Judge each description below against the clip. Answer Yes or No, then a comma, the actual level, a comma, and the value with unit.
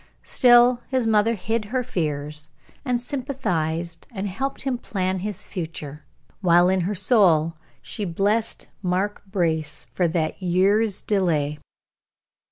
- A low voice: No, high, 190 Hz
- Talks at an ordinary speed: No, slow, 125 wpm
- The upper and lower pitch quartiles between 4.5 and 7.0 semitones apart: Yes, average, 5.2 semitones